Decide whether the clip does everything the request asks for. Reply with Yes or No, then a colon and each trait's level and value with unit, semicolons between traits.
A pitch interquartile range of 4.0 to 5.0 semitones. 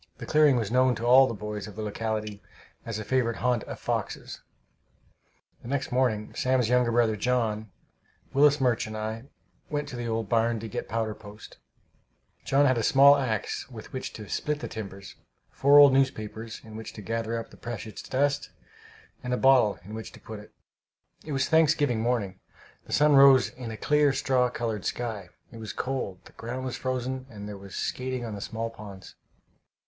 No: average, 3.2 semitones